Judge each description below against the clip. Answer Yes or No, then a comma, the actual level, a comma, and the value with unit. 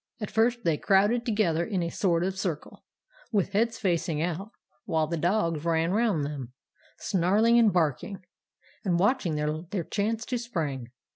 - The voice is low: No, medium, 185 Hz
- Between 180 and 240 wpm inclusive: No, average, 155 wpm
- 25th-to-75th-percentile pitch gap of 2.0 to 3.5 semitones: No, average, 4.8 semitones